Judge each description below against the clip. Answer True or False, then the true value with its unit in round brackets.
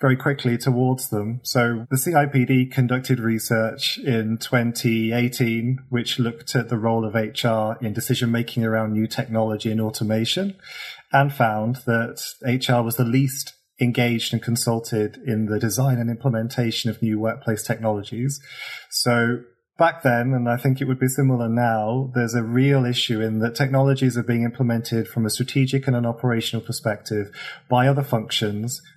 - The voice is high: False (120 Hz)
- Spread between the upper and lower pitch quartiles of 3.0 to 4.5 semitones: False (2.4 semitones)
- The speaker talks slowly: False (155 wpm)